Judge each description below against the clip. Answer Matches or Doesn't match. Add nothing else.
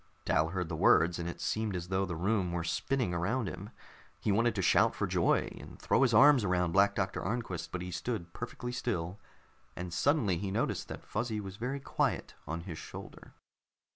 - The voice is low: Matches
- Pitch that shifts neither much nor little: Matches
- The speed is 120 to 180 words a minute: Doesn't match